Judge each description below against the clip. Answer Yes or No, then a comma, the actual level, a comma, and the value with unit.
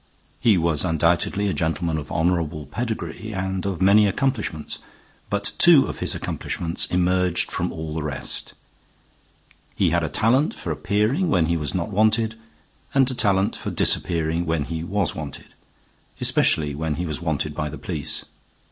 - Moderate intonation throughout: Yes, average, 4.3 semitones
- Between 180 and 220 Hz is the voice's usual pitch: No, very low, 85 Hz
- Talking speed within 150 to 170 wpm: Yes, average, 160 wpm